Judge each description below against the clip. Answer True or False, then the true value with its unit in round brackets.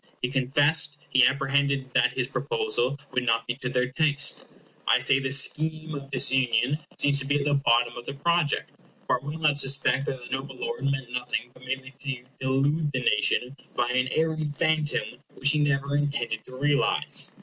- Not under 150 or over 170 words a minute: False (190 wpm)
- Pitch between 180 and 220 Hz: False (140 Hz)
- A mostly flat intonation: True (2.2 semitones)